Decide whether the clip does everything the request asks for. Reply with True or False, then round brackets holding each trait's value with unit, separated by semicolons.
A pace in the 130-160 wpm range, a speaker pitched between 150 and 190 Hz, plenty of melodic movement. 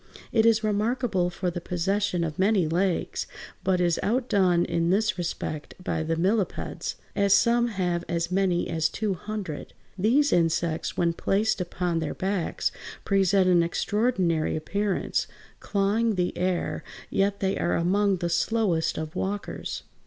False (150 wpm; 185 Hz; 3.1 semitones)